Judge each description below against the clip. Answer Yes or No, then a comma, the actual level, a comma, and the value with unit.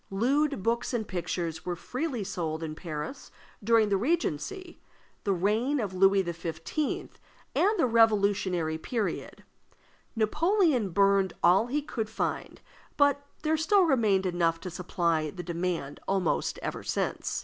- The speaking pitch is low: No, high, 200 Hz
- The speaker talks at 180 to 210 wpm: No, slow, 135 wpm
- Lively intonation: Yes, wide, 6.5 semitones